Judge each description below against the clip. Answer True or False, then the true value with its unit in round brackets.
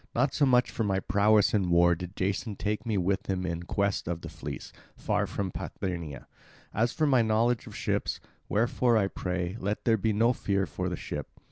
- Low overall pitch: True (100 Hz)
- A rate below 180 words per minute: False (205 wpm)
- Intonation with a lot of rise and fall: False (3.6 semitones)